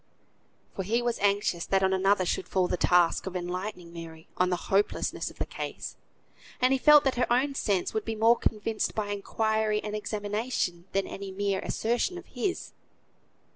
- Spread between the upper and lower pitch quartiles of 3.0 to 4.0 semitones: Yes, average, 3.4 semitones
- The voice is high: Yes, high, 205 Hz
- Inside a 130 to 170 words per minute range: No, average, 180 wpm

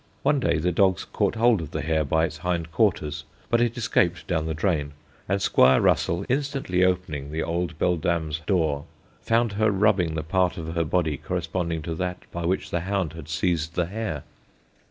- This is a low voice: Yes, very low, 85 Hz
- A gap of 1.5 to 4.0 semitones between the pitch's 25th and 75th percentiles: Yes, average, 3.1 semitones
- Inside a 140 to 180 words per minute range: No, average, 190 wpm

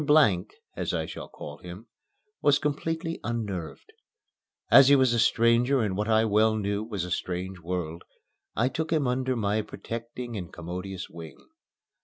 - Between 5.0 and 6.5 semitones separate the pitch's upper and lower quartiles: Yes, wide, 5.5 semitones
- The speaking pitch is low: Yes, low, 110 Hz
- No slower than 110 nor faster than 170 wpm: Yes, average, 160 wpm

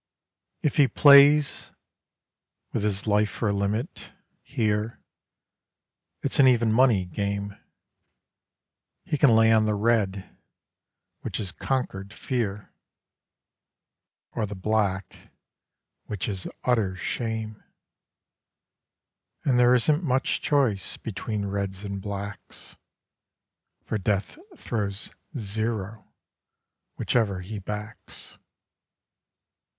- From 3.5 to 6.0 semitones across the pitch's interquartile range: No, average, 3.0 semitones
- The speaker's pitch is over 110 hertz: No, low, 105 Hz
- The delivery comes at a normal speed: No, slow, 95 wpm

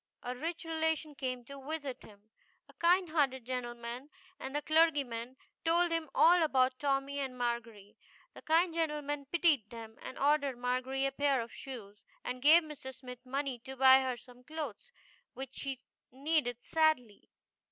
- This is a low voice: No, very high, 270 Hz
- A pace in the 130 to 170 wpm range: Yes, average, 160 wpm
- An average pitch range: Yes, average, 3.7 semitones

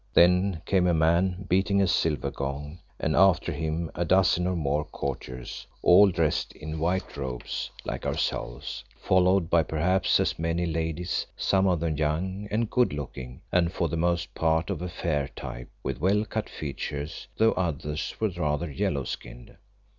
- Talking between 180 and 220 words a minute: No, average, 165 wpm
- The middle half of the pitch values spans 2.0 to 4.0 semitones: Yes, average, 3.4 semitones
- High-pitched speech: No, very low, 85 Hz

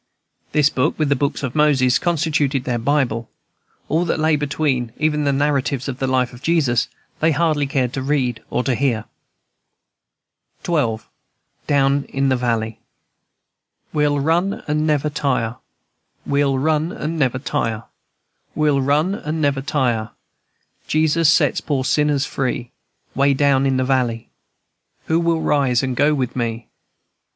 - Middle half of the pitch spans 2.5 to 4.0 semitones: Yes, average, 2.9 semitones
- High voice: No, medium, 140 Hz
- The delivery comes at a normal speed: Yes, average, 145 wpm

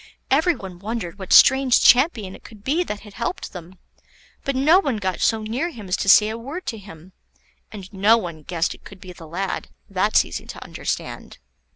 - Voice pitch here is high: Yes, high, 210 Hz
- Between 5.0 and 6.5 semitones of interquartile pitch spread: Yes, wide, 5.5 semitones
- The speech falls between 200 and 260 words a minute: Yes, fast, 205 wpm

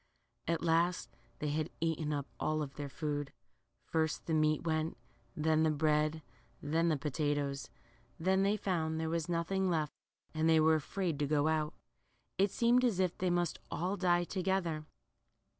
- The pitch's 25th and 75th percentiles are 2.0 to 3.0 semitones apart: Yes, narrow, 2.4 semitones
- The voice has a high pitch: No, medium, 160 Hz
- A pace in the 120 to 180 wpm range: Yes, average, 160 wpm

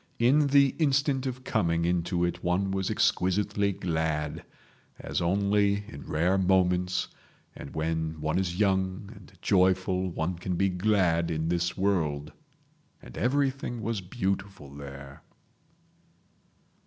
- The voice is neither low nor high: No, very low, 95 Hz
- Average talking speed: No, slow, 120 wpm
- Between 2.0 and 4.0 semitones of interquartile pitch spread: Yes, average, 3.3 semitones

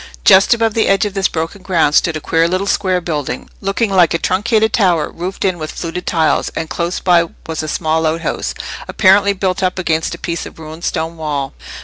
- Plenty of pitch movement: No, average, 3.2 semitones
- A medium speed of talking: No, fast, 210 wpm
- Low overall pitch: No, medium, 175 Hz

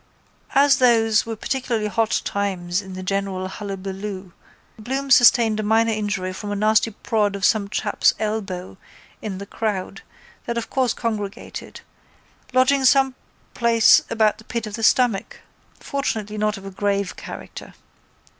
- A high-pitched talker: Yes, high, 215 Hz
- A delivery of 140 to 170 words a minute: Yes, average, 145 wpm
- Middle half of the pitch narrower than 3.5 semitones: Yes, narrow, 2.6 semitones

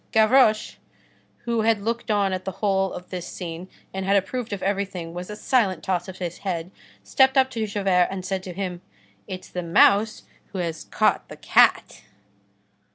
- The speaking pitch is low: No, high, 195 Hz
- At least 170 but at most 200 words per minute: Yes, average, 180 wpm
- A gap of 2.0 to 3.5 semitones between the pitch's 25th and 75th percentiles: Yes, average, 3.0 semitones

